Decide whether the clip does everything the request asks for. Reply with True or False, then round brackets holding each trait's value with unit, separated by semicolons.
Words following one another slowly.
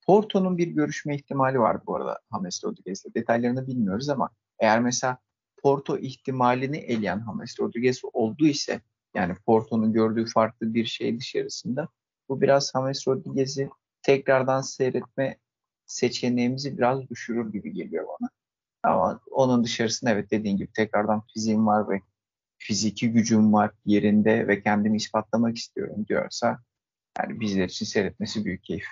False (135 wpm)